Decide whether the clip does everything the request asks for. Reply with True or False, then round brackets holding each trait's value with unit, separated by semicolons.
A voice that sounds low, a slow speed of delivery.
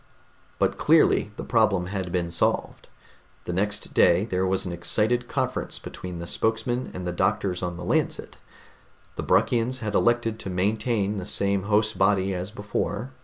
False (100 Hz; 165 wpm)